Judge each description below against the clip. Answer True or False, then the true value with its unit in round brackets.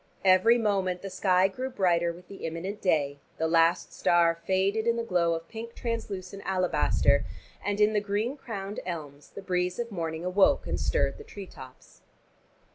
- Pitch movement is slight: False (3.6 semitones)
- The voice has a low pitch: False (190 Hz)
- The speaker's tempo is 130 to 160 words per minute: False (175 wpm)